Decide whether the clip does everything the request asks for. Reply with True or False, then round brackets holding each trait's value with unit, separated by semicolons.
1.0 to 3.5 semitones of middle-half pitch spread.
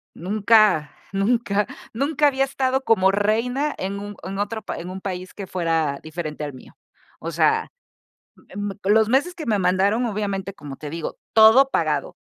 False (4.0 semitones)